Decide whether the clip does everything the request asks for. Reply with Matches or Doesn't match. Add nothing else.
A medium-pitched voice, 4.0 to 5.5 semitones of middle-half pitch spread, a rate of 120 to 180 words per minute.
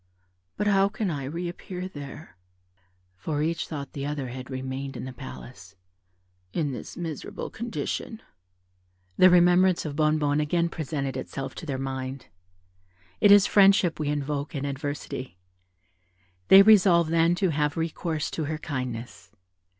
Matches